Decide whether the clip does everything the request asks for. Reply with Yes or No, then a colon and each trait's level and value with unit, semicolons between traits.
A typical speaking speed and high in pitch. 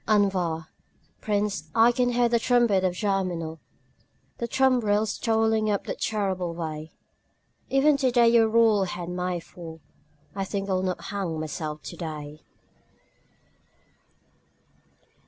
No: slow, 120 wpm; high, 200 Hz